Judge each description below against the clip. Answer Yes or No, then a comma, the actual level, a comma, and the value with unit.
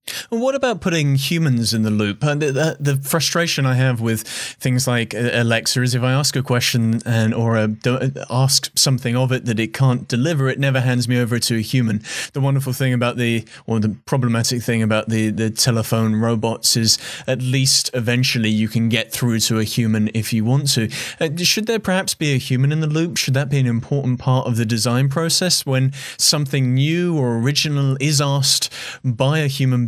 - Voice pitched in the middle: No, low, 130 Hz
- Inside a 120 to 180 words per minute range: No, average, 200 wpm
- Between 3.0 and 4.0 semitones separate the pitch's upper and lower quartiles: Yes, average, 3.3 semitones